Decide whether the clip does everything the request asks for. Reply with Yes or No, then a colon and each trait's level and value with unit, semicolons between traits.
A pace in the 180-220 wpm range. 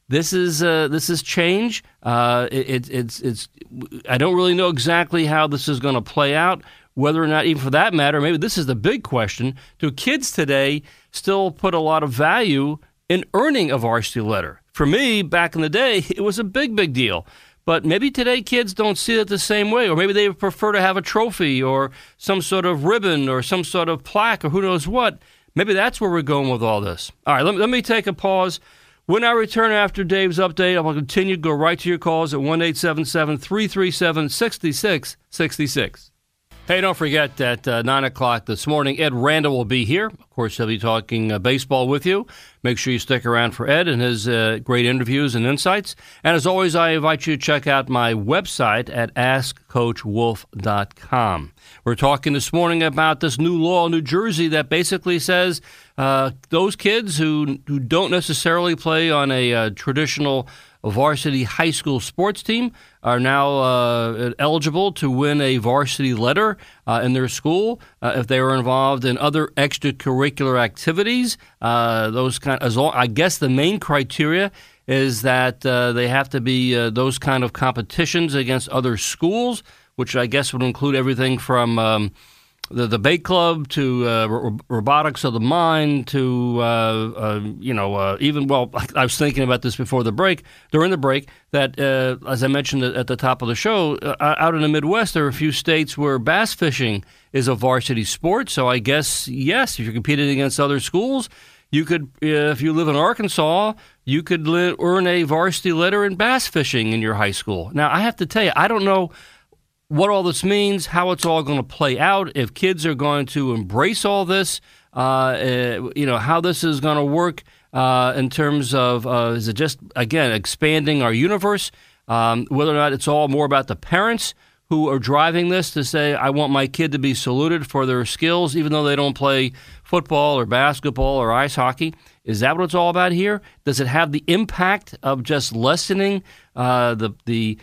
Yes: average, 200 wpm